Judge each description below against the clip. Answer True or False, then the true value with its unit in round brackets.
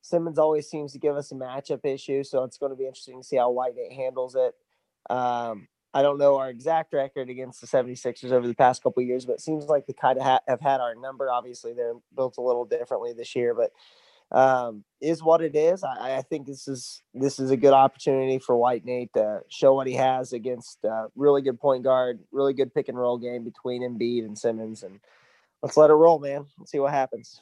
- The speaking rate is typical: False (230 wpm)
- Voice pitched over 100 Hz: True (135 Hz)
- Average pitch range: True (3.8 semitones)